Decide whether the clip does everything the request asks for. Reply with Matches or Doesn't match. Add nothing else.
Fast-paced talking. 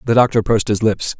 Matches